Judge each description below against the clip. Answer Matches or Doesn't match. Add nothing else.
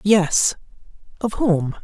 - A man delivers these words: Matches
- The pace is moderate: Doesn't match